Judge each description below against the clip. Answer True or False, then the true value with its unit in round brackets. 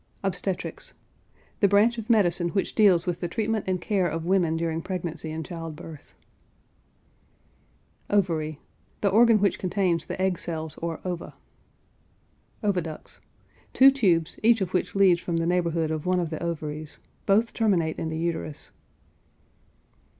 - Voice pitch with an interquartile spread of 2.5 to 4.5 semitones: True (3.4 semitones)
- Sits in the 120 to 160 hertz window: False (175 Hz)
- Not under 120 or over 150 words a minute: True (145 wpm)